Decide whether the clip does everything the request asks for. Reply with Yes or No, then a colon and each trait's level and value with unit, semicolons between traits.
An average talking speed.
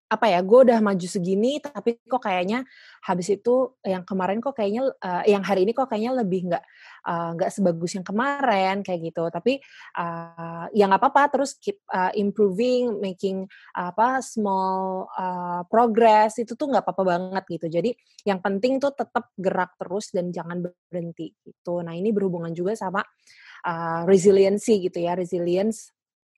No: fast, 160 wpm